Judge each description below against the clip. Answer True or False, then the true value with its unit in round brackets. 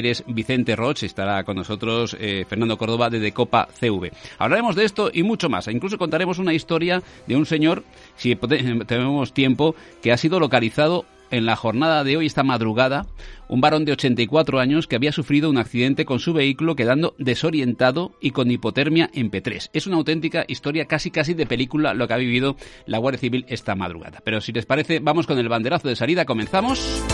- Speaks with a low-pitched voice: True (130 Hz)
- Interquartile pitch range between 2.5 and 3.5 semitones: False (5.3 semitones)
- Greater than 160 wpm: True (190 wpm)